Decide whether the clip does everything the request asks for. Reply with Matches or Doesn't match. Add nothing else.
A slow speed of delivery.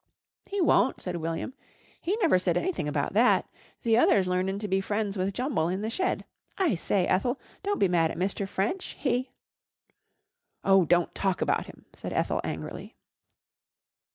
Doesn't match